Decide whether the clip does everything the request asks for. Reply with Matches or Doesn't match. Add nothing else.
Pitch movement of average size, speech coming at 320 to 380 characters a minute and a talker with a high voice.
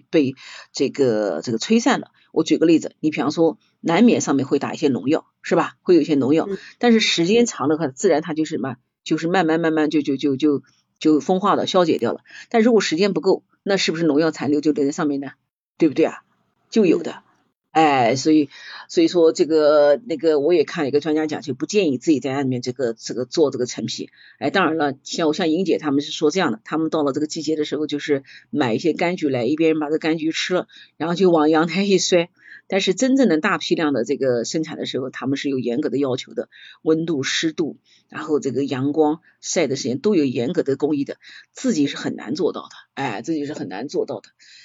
Doesn't match